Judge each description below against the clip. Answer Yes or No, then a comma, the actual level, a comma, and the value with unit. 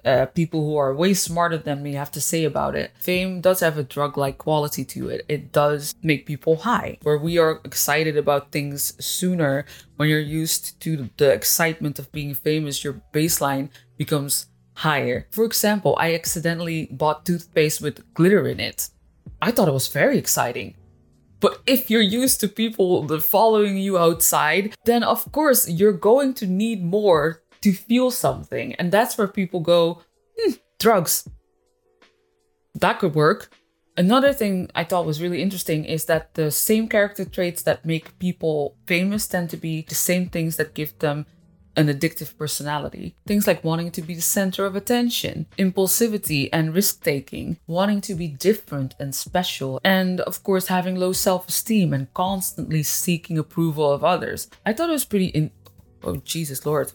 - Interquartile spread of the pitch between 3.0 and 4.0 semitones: No, average, 4.4 semitones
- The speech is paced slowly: No, average, 170 wpm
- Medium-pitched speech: Yes, medium, 165 Hz